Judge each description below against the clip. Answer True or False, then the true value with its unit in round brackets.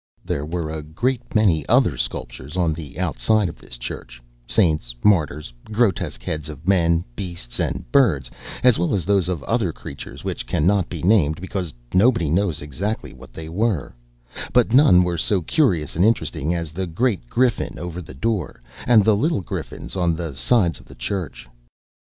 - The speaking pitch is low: True (85 Hz)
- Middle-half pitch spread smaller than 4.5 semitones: False (5.1 semitones)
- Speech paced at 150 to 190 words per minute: True (170 wpm)